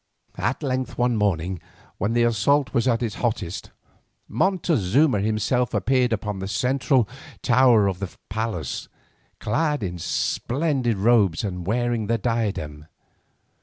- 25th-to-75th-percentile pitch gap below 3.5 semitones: No, average, 4.1 semitones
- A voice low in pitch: Yes, low, 115 Hz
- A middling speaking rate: No, slow, 130 wpm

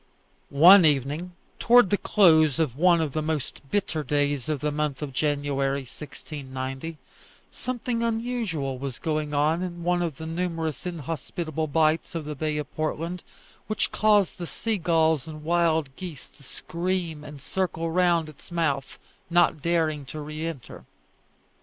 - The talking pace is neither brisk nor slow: Yes, average, 155 wpm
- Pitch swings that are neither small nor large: Yes, average, 3.0 semitones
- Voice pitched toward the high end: No, medium, 160 Hz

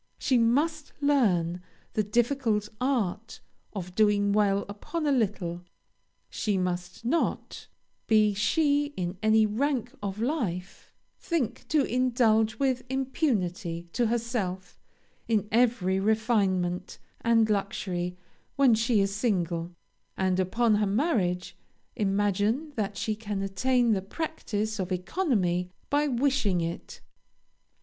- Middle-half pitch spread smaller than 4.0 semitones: No, average, 4.7 semitones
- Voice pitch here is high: Yes, high, 215 Hz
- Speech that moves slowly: Yes, slow, 115 wpm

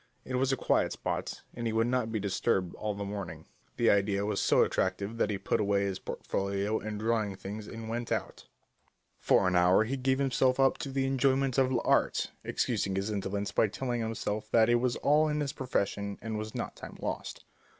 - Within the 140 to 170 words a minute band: No, fast, 205 wpm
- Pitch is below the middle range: Yes, low, 110 Hz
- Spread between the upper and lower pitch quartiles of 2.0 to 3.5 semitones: No, average, 4.1 semitones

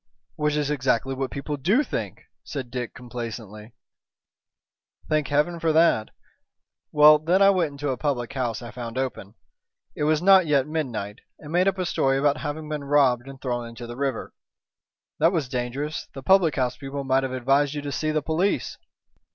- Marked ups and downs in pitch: No, average, 3.5 semitones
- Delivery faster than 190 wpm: No, average, 185 wpm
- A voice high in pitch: No, medium, 140 Hz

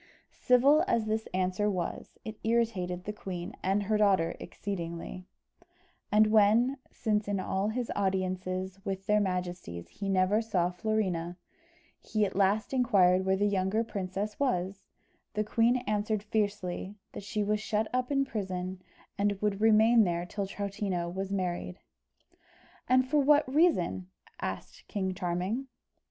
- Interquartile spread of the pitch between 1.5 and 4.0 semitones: Yes, average, 2.8 semitones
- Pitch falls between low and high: No, high, 200 Hz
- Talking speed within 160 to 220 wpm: No, average, 145 wpm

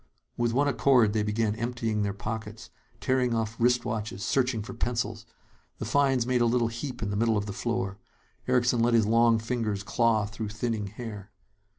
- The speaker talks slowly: No, average, 180 wpm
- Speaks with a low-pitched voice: Yes, low, 115 Hz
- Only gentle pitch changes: Yes, narrow, 2.2 semitones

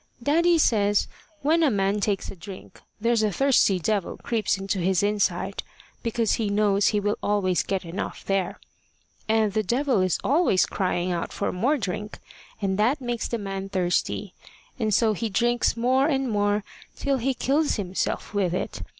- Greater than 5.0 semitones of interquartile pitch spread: No, average, 3.7 semitones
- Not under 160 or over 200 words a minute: Yes, average, 170 wpm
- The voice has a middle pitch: No, high, 210 Hz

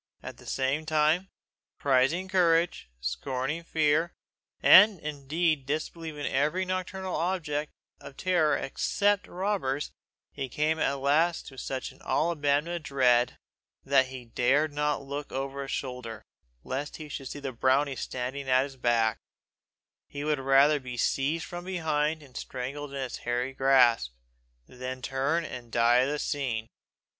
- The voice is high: No, medium, 140 Hz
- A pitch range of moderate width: Yes, average, 3.2 semitones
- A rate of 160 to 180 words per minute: No, average, 150 wpm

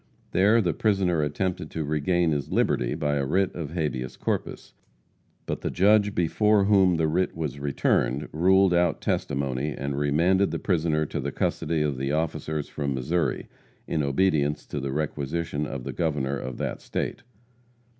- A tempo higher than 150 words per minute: Yes, average, 165 wpm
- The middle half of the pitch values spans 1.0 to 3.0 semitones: No, average, 4.0 semitones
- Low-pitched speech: Yes, very low, 80 Hz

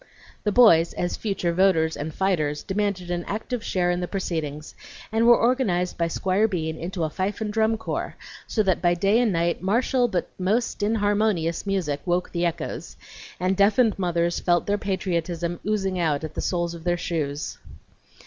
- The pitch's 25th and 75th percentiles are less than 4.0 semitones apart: Yes, average, 3.4 semitones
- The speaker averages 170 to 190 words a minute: Yes, average, 175 wpm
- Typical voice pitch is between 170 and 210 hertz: Yes, medium, 185 Hz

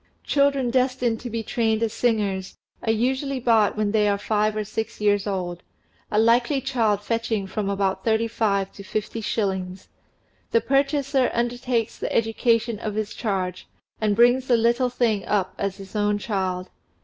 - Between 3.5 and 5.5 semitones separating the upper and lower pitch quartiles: No, average, 2.9 semitones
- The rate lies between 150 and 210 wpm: Yes, average, 165 wpm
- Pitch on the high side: Yes, high, 220 Hz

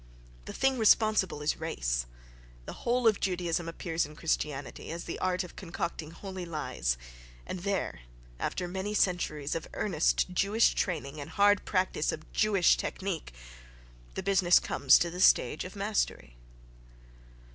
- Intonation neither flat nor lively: Yes, average, 4.2 semitones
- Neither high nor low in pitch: Yes, medium, 180 Hz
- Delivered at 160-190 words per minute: No, average, 145 wpm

